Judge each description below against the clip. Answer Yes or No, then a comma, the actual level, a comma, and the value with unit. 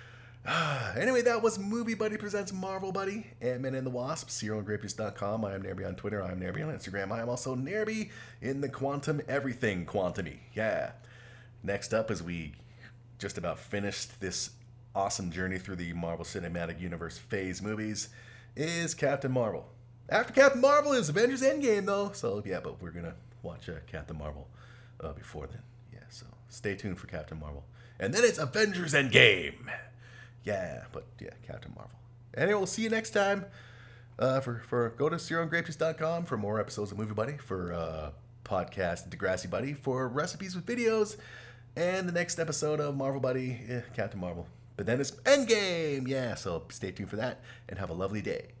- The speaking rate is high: No, average, 180 wpm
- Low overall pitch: Yes, low, 120 Hz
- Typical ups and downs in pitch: No, wide, 7.2 semitones